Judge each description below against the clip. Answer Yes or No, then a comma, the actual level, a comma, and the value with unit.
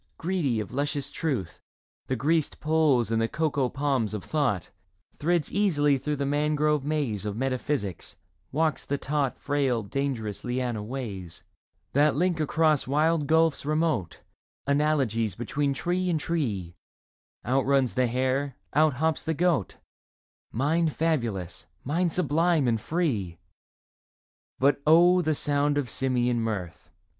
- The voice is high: No, medium, 140 Hz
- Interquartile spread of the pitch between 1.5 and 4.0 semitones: No, average, 4.4 semitones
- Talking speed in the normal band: No, slow, 130 wpm